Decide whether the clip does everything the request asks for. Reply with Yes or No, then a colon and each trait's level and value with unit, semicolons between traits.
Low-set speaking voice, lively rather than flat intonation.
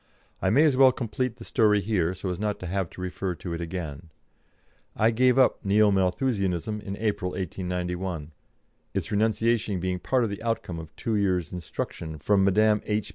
No: low, 100 Hz; average, 3.4 semitones